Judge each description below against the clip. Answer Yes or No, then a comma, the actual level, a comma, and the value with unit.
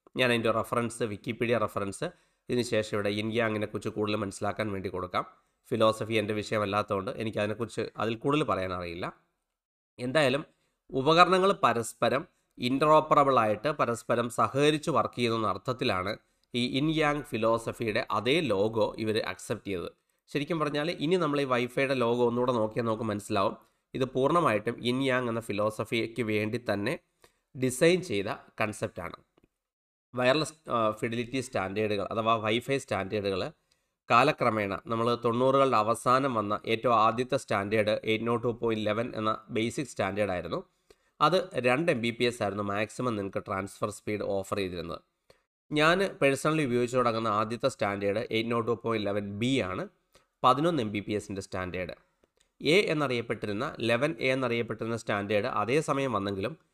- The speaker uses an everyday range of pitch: Yes, average, 3.7 semitones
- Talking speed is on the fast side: Yes, fast, 130 wpm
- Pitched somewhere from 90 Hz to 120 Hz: Yes, low, 115 Hz